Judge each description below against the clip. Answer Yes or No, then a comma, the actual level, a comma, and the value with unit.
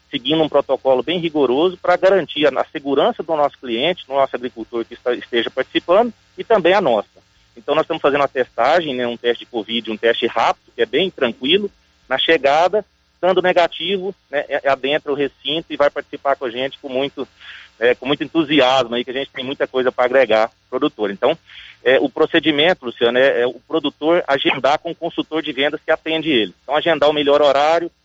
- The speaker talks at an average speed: No, fast, 210 wpm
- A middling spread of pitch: Yes, average, 4.1 semitones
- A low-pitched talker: No, medium, 145 Hz